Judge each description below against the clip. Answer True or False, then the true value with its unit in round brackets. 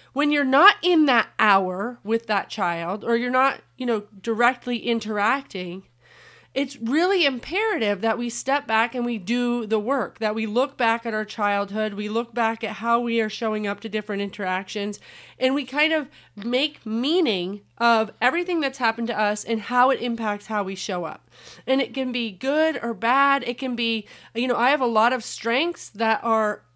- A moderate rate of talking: True (195 wpm)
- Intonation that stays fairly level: False (3.4 semitones)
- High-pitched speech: True (230 Hz)